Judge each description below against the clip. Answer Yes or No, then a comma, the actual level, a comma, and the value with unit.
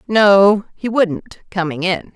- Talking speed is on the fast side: No, average, 140 wpm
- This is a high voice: Yes, high, 195 Hz